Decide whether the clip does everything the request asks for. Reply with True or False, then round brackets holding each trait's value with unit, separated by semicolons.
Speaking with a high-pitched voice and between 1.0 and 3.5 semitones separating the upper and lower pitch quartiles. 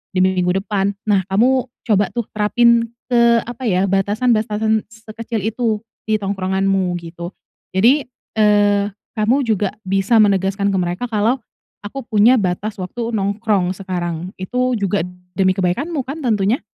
True (205 Hz; 3.2 semitones)